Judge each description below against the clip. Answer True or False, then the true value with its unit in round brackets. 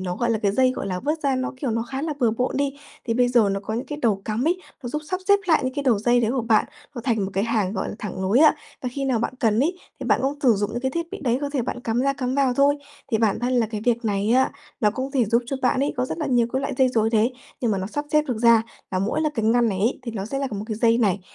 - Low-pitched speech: False (240 Hz)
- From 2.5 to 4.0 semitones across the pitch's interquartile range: True (3.6 semitones)